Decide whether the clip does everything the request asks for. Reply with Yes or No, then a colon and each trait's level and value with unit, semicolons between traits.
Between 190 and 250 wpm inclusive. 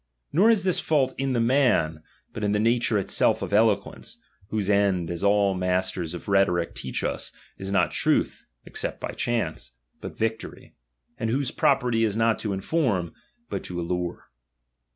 No: average, 175 wpm